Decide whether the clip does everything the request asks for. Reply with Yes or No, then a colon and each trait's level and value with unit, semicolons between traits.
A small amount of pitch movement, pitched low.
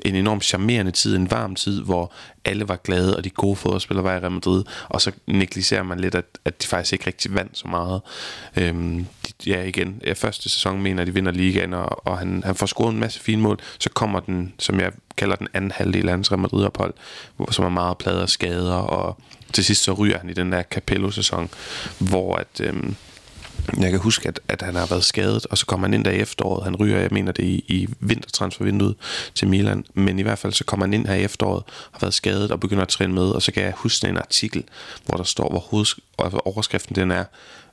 Yes: narrow, 2.3 semitones; very low, 95 Hz